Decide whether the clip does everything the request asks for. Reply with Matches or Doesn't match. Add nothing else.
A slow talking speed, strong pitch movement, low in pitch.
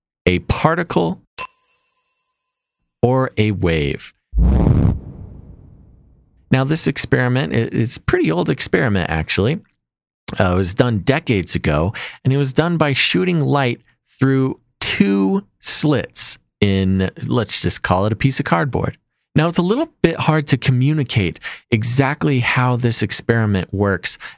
Matches